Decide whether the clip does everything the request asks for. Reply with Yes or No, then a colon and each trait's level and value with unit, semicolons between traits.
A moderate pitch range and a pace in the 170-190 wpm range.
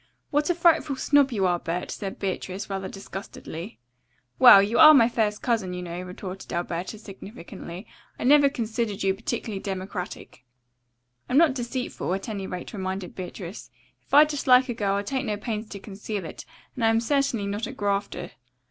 Yes: average, 4.3 semitones; average, 175 wpm